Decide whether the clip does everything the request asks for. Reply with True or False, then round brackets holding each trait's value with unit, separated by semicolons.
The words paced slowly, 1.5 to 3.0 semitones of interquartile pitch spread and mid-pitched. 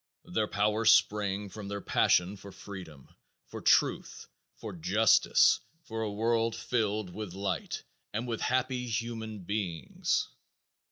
False (125 wpm; 2.4 semitones; 105 Hz)